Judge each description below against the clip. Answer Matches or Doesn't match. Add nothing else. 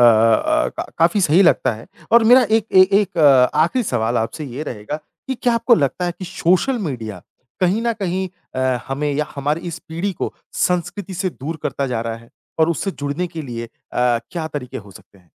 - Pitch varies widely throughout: Matches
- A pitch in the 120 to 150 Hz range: Doesn't match